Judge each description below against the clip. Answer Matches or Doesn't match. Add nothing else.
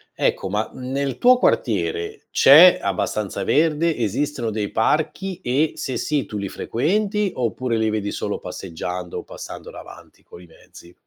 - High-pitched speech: Doesn't match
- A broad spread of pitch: Matches